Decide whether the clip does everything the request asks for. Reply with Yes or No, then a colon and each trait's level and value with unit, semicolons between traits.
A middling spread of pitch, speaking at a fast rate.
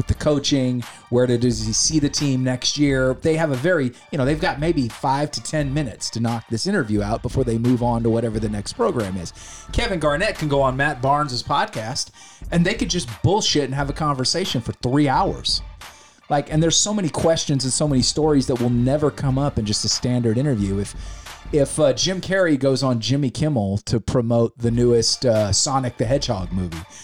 Yes: average, 4.2 semitones; fast, 215 wpm